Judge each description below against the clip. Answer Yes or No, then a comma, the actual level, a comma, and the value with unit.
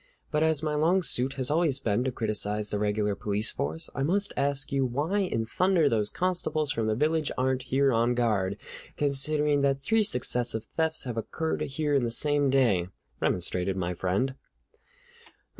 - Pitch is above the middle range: No, low, 135 Hz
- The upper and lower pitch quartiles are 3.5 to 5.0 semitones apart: No, wide, 5.6 semitones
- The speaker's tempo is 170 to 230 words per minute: Yes, average, 175 wpm